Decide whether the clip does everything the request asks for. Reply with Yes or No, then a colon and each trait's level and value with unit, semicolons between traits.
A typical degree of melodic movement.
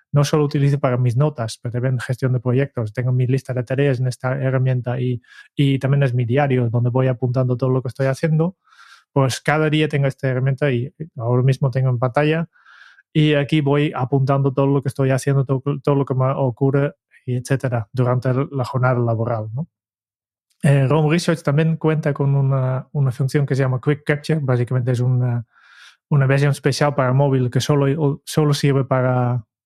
No: narrow, 2.2 semitones